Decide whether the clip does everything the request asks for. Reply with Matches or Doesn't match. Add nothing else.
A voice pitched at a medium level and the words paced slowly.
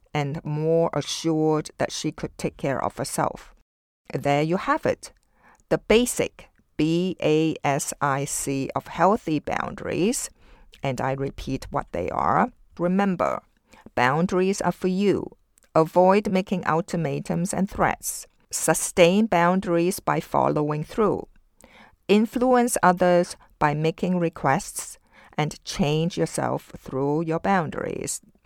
Matches